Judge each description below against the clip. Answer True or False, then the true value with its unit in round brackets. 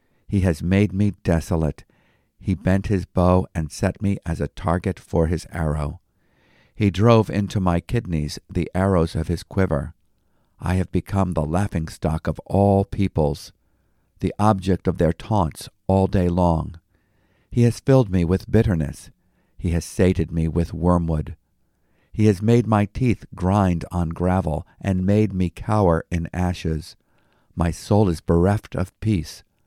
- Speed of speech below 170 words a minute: True (155 wpm)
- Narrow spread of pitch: False (3.2 semitones)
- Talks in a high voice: False (90 Hz)